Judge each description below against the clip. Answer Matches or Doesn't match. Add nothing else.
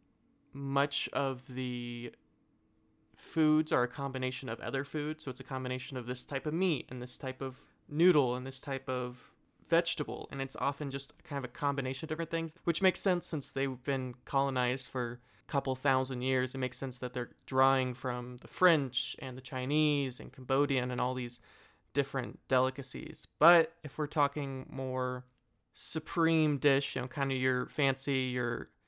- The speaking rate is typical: Matches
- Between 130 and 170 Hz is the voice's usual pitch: Matches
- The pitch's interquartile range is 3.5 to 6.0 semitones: Doesn't match